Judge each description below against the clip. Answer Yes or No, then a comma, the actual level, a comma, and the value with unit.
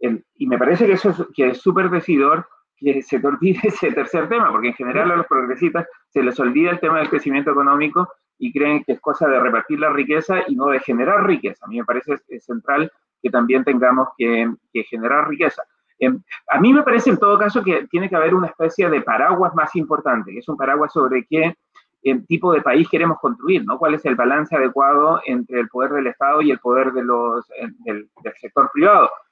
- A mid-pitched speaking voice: Yes, medium, 150 Hz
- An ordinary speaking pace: No, fast, 225 wpm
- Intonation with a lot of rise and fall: Yes, wide, 6.2 semitones